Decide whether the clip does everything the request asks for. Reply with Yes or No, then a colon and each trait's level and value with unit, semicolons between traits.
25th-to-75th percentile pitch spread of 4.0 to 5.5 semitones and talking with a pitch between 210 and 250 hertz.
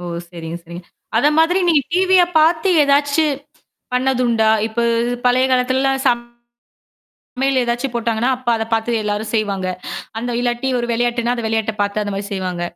No: average, 3.3 semitones; high, 240 Hz